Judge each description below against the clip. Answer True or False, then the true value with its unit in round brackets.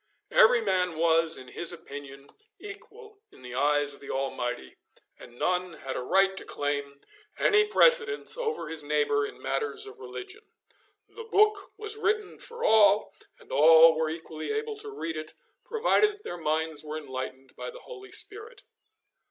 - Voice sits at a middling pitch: True (175 Hz)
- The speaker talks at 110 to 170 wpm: True (165 wpm)